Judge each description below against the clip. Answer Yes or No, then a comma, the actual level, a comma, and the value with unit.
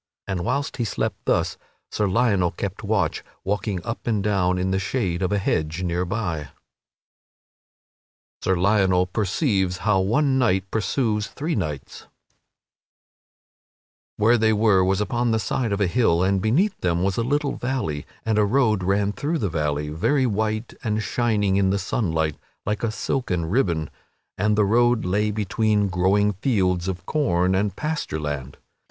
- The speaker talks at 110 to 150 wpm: No, average, 160 wpm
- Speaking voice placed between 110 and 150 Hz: No, low, 100 Hz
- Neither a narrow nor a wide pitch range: Yes, average, 3.6 semitones